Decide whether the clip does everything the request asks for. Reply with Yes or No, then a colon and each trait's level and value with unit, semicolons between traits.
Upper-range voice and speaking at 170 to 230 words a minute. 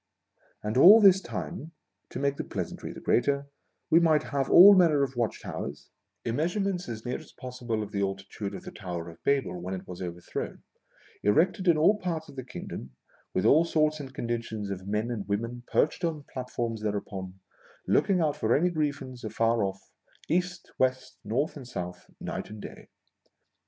No: low, 125 Hz; average, 185 wpm